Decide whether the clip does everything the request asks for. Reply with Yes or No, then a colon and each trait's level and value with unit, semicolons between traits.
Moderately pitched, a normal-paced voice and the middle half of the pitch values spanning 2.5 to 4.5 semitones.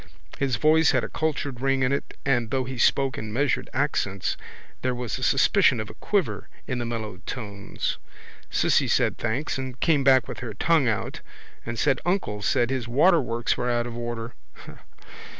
No: low, 125 Hz; average, 180 wpm; average, 2.9 semitones